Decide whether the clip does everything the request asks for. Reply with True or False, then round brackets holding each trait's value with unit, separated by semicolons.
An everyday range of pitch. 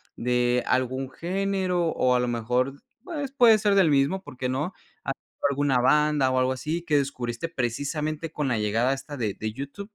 True (5.0 semitones)